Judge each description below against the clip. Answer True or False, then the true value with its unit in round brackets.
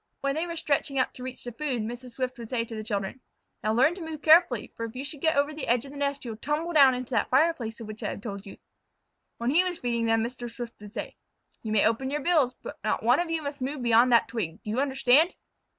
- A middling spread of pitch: True (4.2 semitones)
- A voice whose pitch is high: True (255 Hz)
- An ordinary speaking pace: False (275 wpm)